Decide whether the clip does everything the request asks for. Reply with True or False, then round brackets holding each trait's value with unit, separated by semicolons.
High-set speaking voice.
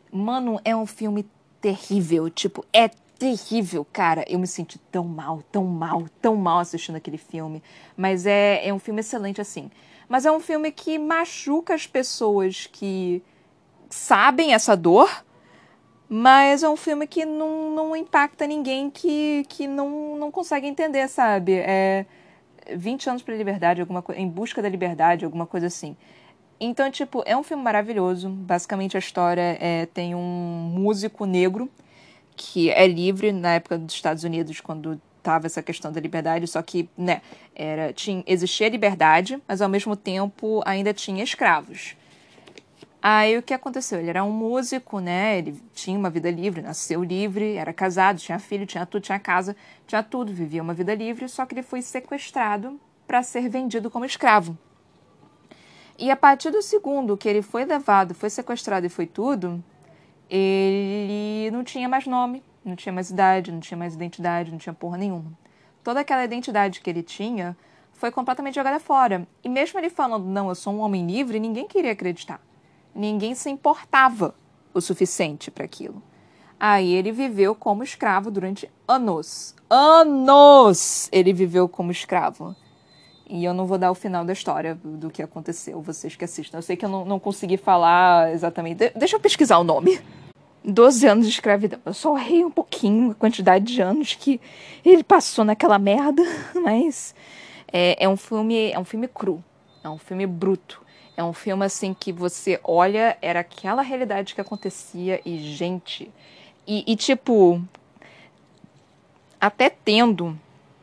True (200 Hz)